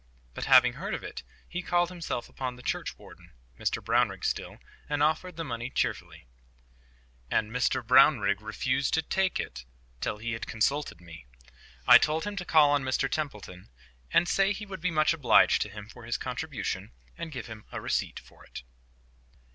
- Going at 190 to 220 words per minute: No, average, 170 wpm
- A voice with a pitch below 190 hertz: Yes, low, 135 Hz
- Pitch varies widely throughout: Yes, wide, 7.0 semitones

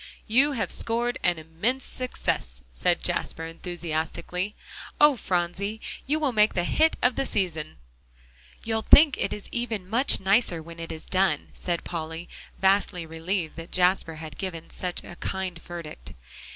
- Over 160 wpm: No, average, 150 wpm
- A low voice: No, medium, 185 Hz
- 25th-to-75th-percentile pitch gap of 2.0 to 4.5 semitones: No, average, 5.2 semitones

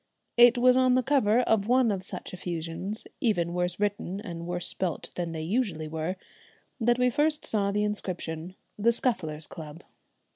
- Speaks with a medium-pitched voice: No, high, 200 Hz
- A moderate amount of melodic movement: No, wide, 5.8 semitones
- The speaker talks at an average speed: Yes, average, 170 wpm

